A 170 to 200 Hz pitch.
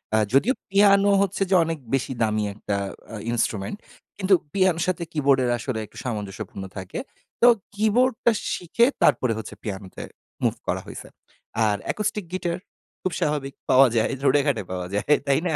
No: medium, 140 Hz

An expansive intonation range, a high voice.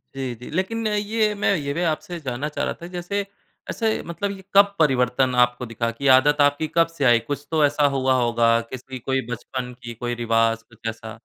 No: wide, 5.9 semitones; low, 135 Hz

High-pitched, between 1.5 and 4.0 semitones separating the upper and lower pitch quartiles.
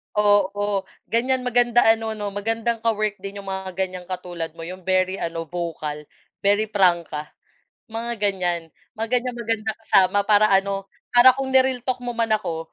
Yes: high, 205 Hz; average, 3.6 semitones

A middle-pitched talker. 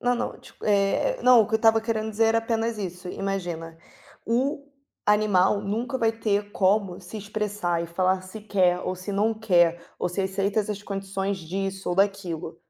No: high, 200 Hz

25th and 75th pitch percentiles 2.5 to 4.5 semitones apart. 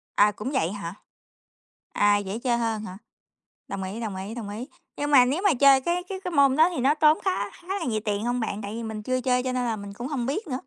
No: average, 5.1 semitones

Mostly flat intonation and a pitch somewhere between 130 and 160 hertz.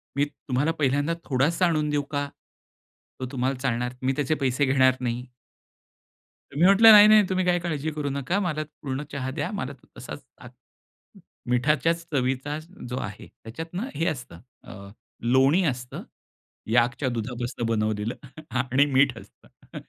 No: average, 3.8 semitones; low, 135 Hz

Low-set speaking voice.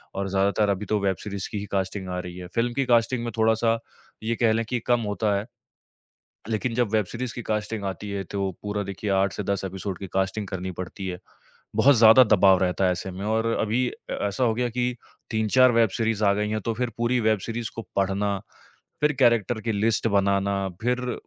Yes: low, 105 Hz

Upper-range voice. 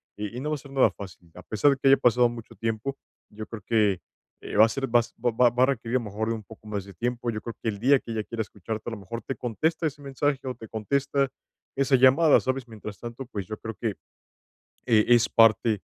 No: low, 115 Hz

